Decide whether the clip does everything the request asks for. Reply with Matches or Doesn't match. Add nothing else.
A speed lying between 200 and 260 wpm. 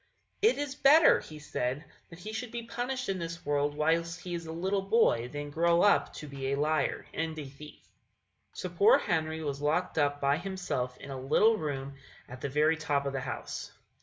Matches